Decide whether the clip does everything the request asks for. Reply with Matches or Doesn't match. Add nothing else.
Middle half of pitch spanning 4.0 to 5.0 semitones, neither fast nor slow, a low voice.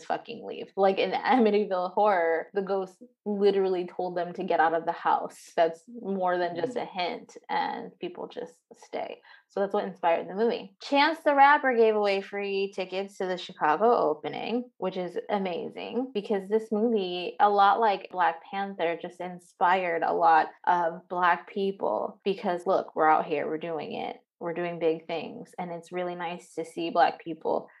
Doesn't match